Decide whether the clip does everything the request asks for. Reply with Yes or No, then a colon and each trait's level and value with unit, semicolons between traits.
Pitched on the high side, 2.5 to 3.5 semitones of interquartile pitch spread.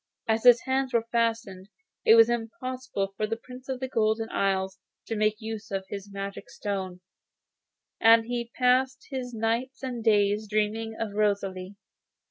Yes: high, 225 Hz; average, 3.2 semitones